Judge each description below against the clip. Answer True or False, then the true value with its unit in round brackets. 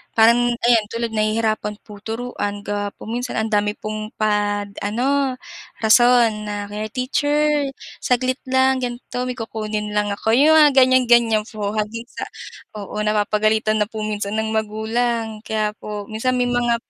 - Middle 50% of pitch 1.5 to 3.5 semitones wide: True (2.5 semitones)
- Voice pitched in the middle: False (220 Hz)